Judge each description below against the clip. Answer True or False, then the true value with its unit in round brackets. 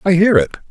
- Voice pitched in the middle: True (175 Hz)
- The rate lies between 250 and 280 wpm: True (255 wpm)